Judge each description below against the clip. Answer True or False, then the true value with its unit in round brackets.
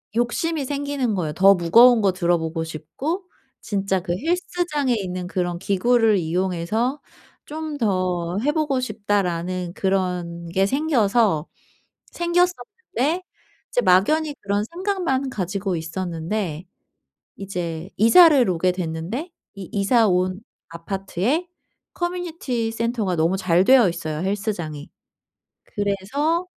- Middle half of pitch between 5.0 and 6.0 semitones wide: False (7.2 semitones)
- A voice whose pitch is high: True (200 Hz)